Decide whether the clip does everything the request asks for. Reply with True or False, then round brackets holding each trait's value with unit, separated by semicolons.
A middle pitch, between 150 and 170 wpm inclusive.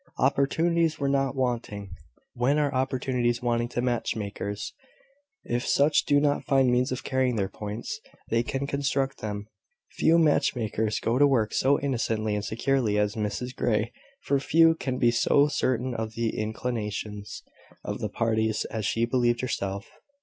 False (120 Hz; 160 wpm)